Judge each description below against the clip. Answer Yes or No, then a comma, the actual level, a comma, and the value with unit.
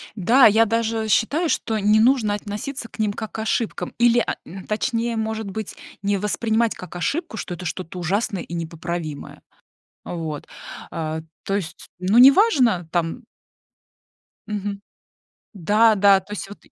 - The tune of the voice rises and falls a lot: No, average, 3.7 semitones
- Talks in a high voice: Yes, high, 210 Hz